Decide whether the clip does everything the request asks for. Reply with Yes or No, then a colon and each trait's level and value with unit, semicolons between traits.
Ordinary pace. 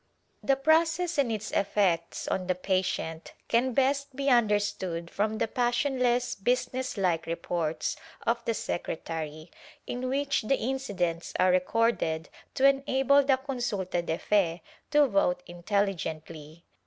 No: slow, 130 wpm